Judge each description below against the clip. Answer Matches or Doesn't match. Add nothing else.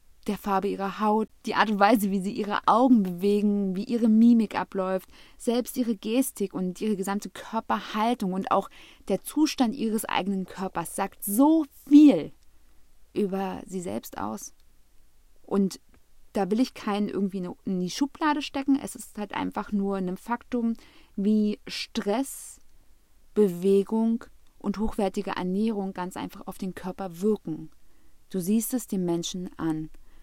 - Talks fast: Doesn't match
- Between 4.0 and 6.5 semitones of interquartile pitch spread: Doesn't match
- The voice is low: Doesn't match